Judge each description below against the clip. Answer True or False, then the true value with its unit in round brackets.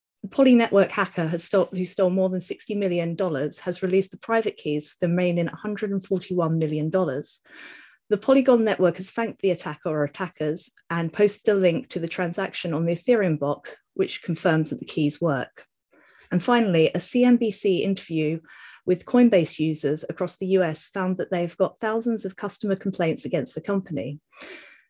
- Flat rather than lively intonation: False (3.3 semitones)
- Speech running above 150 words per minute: True (170 wpm)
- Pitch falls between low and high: True (180 Hz)